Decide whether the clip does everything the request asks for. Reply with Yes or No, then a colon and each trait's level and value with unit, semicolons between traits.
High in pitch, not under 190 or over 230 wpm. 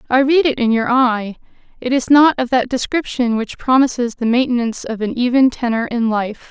Yes: high, 245 Hz; fast, 205 wpm